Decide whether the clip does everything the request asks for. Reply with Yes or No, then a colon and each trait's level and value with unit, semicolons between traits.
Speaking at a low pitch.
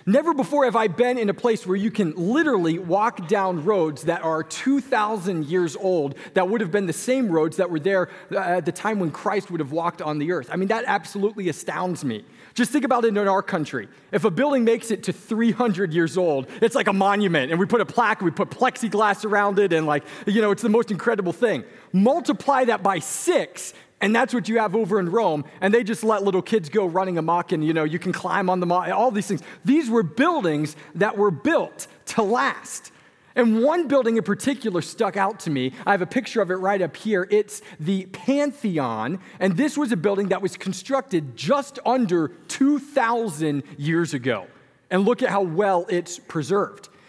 No: high, 200 Hz